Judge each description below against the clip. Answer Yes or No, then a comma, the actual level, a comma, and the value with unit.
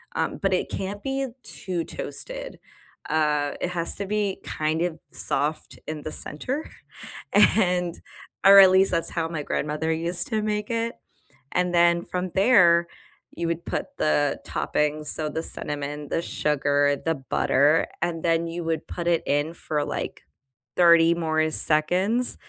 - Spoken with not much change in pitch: No, average, 3.3 semitones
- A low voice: No, medium, 170 Hz